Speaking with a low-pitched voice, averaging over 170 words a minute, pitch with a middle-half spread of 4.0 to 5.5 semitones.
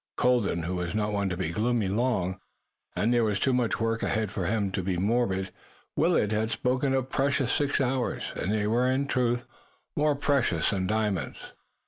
Yes: low, 110 Hz; average, 185 wpm; average, 4.5 semitones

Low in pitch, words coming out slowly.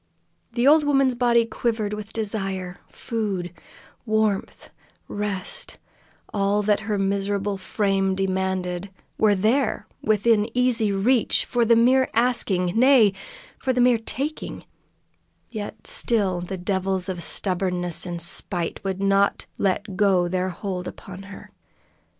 No: high, 200 Hz; slow, 125 wpm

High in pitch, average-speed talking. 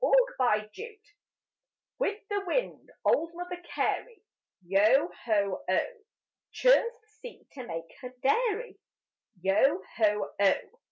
No: very high, 345 Hz; slow, 115 wpm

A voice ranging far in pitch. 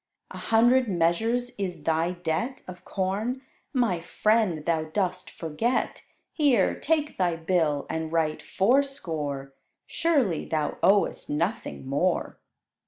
Yes: wide, 6.5 semitones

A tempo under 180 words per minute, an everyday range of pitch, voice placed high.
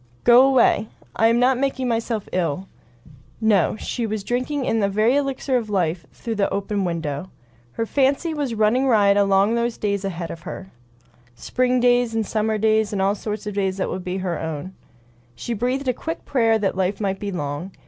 No: average, 195 wpm; average, 4.1 semitones; high, 215 Hz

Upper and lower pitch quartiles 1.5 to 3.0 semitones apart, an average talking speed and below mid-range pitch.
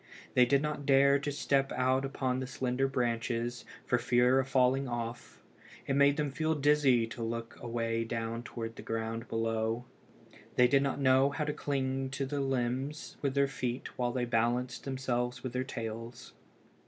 Yes: narrow, 2.5 semitones; average, 175 wpm; low, 130 Hz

